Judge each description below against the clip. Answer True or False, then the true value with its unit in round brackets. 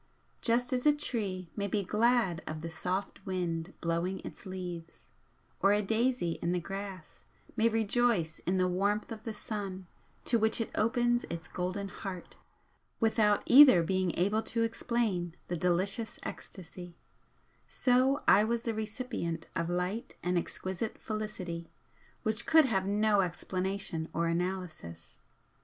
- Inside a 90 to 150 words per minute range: True (145 wpm)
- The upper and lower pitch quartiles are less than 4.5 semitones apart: True (4.1 semitones)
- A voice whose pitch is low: False (195 Hz)